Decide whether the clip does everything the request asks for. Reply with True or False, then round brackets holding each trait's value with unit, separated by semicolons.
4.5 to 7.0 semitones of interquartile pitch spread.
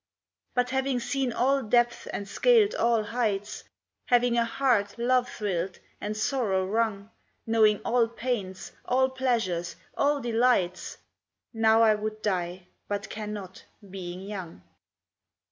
False (3.7 semitones)